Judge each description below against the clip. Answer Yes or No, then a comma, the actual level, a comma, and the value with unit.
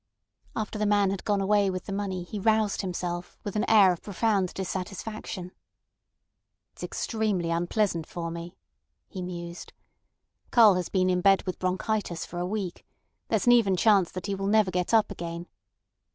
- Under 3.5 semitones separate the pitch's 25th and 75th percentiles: Yes, average, 2.8 semitones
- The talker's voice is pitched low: No, high, 190 Hz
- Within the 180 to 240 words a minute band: No, average, 170 wpm